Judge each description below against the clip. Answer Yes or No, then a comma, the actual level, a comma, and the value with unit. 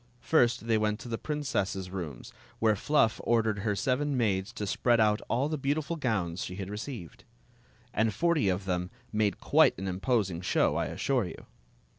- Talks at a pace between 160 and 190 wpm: Yes, average, 175 wpm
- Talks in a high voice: No, low, 110 Hz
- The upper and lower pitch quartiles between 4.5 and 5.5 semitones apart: Yes, average, 4.9 semitones